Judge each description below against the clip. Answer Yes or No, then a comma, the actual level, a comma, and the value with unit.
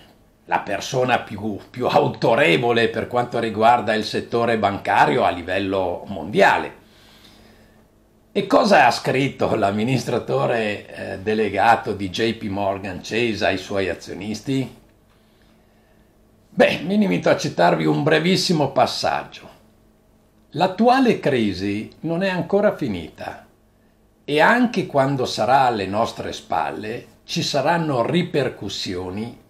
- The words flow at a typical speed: No, slow, 105 wpm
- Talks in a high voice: No, low, 110 Hz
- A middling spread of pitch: Yes, average, 4.6 semitones